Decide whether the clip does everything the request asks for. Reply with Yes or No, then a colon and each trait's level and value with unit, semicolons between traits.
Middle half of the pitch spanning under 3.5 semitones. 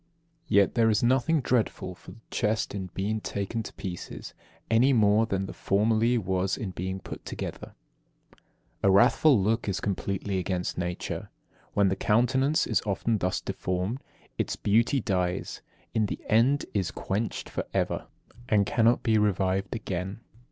Yes: average, 3.1 semitones